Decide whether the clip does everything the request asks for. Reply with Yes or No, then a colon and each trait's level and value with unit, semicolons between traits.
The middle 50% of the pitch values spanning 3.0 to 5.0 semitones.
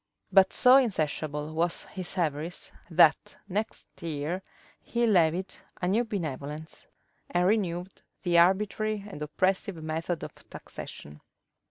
Yes: average, 3.9 semitones